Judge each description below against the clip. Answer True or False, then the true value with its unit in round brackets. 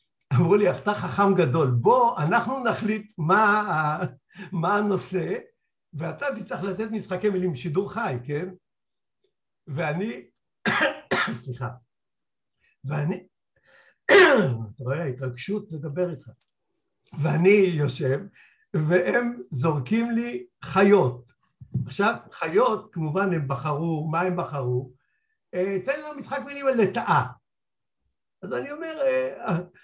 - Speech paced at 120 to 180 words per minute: False (100 wpm)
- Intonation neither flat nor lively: False (6.4 semitones)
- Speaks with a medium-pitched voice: True (180 Hz)